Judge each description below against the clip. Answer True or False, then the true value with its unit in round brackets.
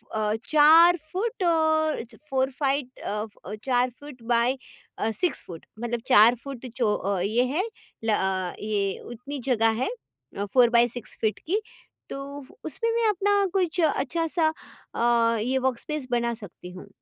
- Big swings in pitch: True (6.1 semitones)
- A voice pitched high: True (255 Hz)